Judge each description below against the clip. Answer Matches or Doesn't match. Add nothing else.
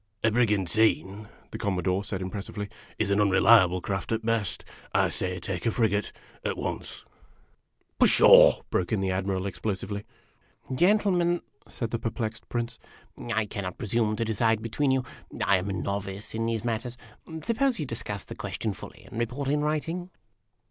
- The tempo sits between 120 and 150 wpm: Doesn't match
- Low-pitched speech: Matches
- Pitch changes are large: Doesn't match